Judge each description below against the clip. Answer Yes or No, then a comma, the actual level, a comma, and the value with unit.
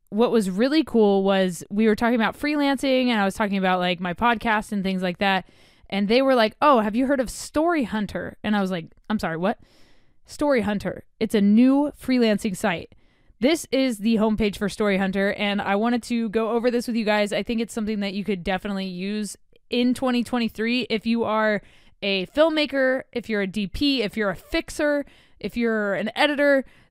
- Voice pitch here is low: No, high, 220 Hz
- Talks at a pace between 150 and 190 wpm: No, fast, 205 wpm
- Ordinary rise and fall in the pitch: Yes, average, 3.6 semitones